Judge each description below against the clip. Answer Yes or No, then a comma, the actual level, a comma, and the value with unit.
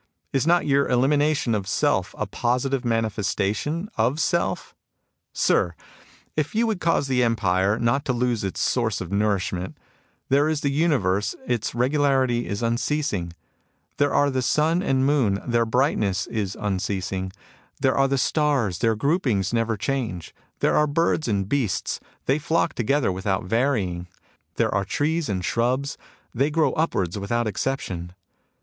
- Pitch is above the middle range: No, low, 120 Hz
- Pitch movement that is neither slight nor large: No, wide, 6.0 semitones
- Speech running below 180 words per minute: Yes, average, 150 wpm